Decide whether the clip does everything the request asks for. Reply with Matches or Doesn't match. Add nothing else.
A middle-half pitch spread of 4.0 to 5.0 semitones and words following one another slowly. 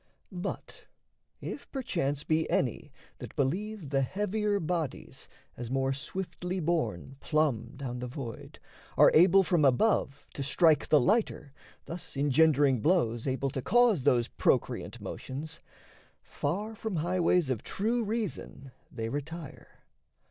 Doesn't match